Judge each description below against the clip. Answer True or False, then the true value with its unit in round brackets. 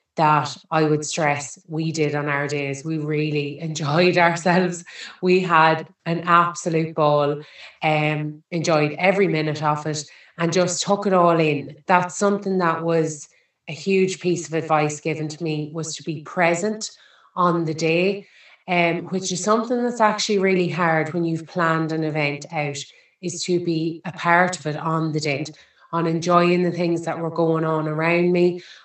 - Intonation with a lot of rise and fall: False (2.4 semitones)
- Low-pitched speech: False (165 Hz)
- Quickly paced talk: False (175 wpm)